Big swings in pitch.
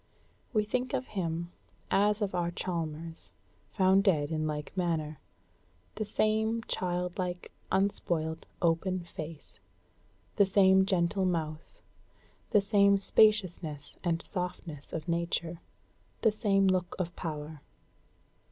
No: average, 3.3 semitones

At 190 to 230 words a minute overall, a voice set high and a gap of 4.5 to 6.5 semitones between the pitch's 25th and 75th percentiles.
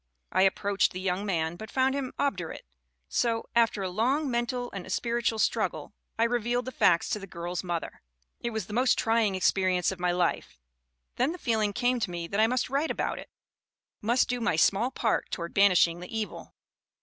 Yes: average, 195 wpm; high, 215 Hz; average, 4.8 semitones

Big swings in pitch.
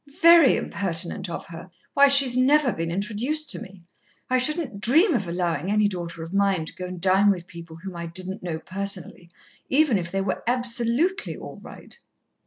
Yes: wide, 6.5 semitones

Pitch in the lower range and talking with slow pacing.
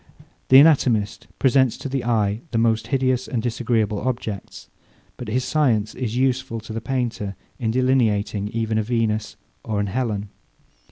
No: low, 115 Hz; average, 155 wpm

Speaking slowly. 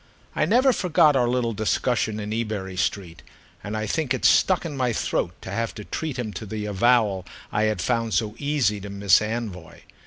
No: average, 195 wpm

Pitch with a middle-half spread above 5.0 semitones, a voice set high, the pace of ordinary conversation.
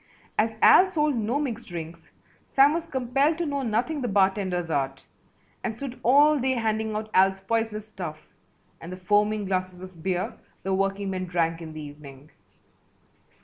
Yes: wide, 5.6 semitones; high, 210 Hz; average, 160 wpm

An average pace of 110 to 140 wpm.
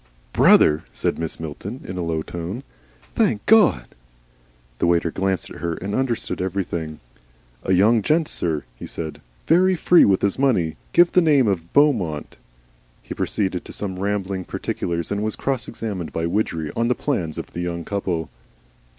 No: average, 165 wpm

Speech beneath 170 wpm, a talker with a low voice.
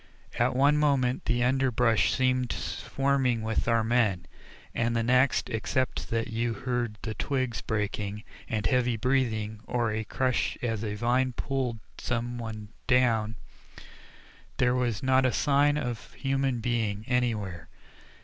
Yes: average, 140 wpm; low, 120 Hz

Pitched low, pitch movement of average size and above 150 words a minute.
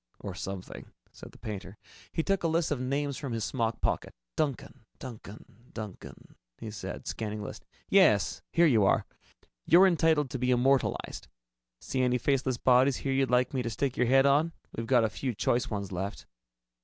Yes: low, 125 Hz; average, 4.0 semitones; average, 185 wpm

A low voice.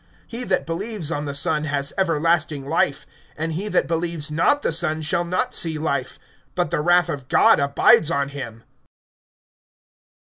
No: medium, 160 Hz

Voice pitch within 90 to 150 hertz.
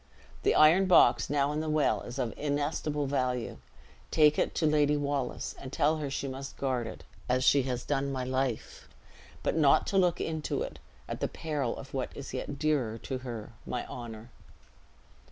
Yes: medium, 140 Hz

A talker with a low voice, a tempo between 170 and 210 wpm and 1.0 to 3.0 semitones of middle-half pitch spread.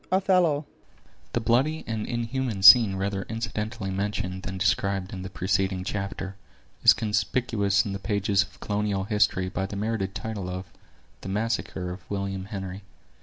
No: low, 100 Hz; average, 150 wpm; average, 2.7 semitones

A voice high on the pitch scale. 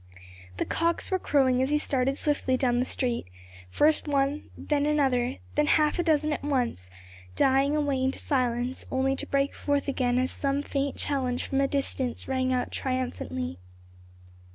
Yes: very high, 270 Hz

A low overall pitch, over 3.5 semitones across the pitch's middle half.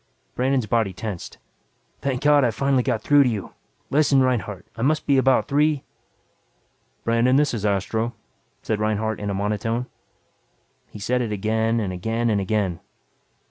Yes: low, 115 Hz; average, 3.9 semitones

